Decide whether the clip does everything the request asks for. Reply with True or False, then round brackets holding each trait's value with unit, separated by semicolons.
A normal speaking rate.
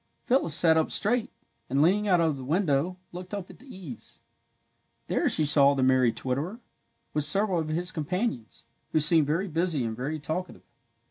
True (180 wpm)